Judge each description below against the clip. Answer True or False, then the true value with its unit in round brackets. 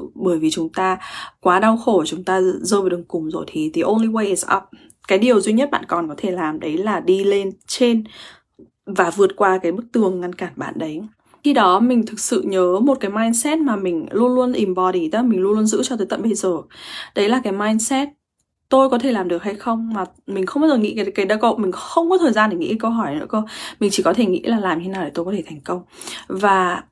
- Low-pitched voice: False (205 Hz)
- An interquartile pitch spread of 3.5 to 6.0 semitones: True (4.0 semitones)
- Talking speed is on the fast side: True (260 wpm)